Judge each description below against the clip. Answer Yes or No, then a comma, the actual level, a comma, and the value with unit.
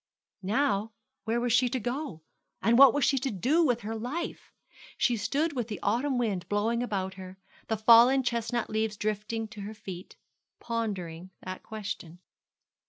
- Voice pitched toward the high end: Yes, high, 225 Hz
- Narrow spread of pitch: No, average, 3.2 semitones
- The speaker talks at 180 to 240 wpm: No, average, 165 wpm